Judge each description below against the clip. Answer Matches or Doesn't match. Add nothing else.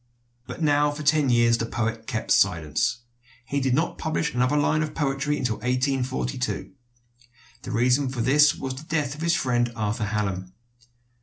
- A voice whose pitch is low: Matches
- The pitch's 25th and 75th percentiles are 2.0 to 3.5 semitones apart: Doesn't match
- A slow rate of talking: Doesn't match